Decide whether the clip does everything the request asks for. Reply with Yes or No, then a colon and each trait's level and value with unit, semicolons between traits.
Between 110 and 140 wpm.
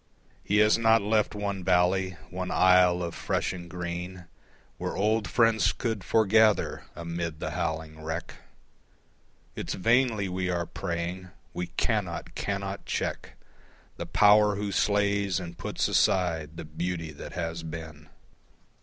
Yes: slow, 135 wpm